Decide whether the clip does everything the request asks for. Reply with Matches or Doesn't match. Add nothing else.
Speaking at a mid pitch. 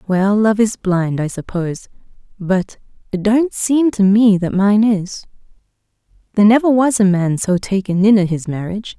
Doesn't match